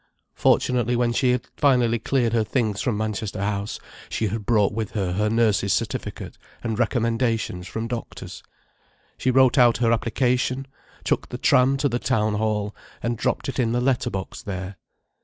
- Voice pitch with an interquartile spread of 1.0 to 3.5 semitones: Yes, average, 2.8 semitones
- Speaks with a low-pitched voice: Yes, low, 115 Hz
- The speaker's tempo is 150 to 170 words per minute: Yes, average, 165 wpm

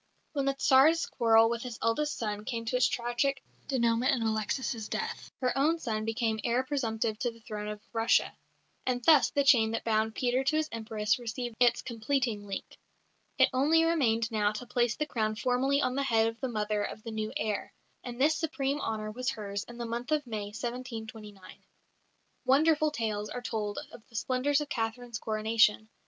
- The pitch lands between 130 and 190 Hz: No, high, 235 Hz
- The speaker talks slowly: No, average, 190 wpm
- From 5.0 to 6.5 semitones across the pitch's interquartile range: No, average, 3.2 semitones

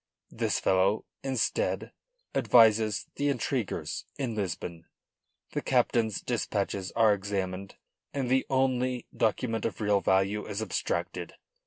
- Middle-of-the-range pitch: No, low, 110 Hz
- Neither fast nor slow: No, slow, 115 wpm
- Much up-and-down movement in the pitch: No, average, 4.1 semitones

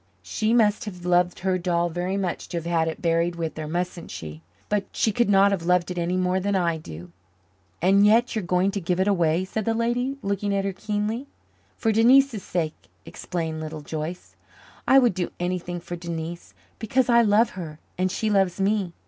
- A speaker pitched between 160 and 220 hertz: Yes, medium, 185 Hz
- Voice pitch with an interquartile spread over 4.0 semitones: No, average, 3.4 semitones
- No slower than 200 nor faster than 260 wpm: Yes, fast, 205 wpm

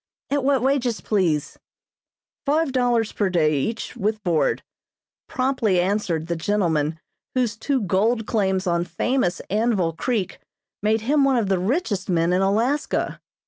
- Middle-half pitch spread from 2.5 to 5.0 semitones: No, wide, 5.6 semitones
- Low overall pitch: No, high, 210 Hz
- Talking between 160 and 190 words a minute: No, average, 140 wpm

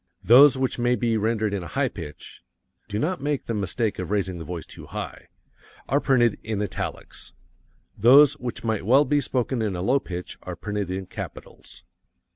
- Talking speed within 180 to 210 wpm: Yes, average, 185 wpm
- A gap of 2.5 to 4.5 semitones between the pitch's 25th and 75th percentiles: No, average, 4.9 semitones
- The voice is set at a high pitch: No, low, 110 Hz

